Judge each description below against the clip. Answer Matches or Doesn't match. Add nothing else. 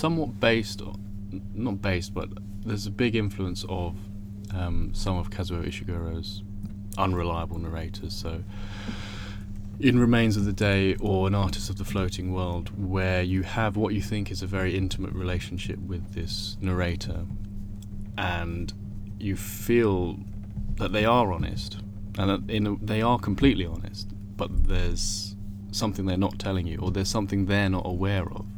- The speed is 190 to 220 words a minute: Doesn't match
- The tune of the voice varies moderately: Doesn't match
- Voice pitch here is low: Matches